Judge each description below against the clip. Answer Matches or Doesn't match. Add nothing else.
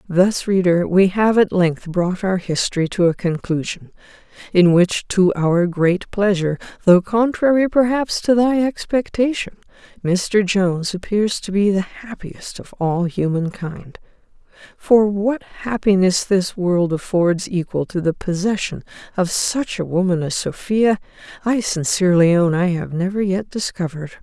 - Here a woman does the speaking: Matches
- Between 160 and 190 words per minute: Doesn't match